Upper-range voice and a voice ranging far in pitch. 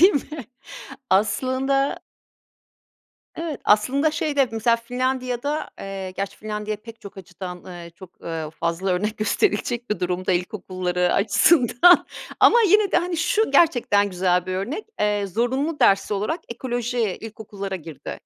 Yes: high, 215 Hz; wide, 6.0 semitones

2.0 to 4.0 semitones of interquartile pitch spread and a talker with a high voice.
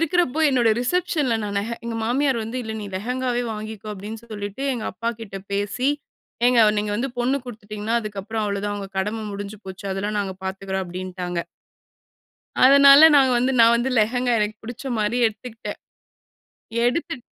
Yes: average, 3.5 semitones; high, 220 Hz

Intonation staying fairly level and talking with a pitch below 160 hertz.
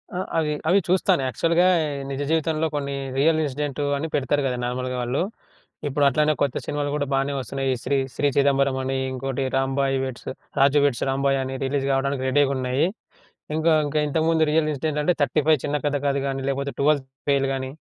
Yes: narrow, 1.9 semitones; medium, 140 Hz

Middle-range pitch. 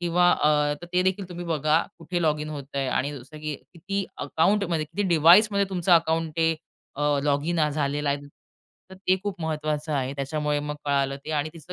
Yes: medium, 155 Hz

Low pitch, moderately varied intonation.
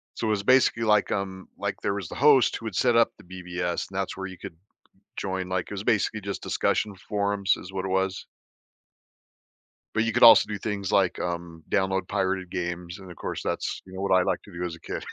No: very low, 95 Hz; narrow, 2.2 semitones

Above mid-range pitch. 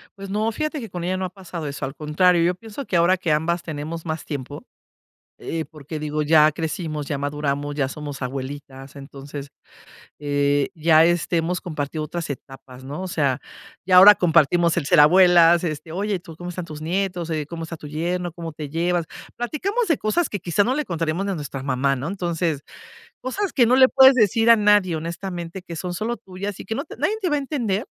No: medium, 170 Hz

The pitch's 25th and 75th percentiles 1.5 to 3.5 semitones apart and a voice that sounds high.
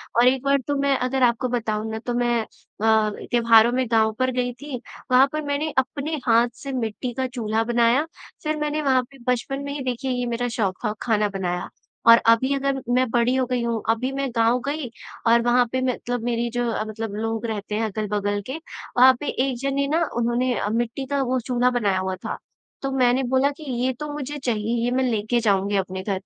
Yes: average, 2.8 semitones; high, 245 Hz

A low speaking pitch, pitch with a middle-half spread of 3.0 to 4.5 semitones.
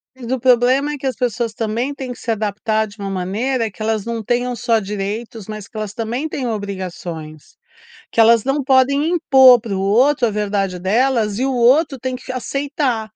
No: high, 230 Hz; average, 3.7 semitones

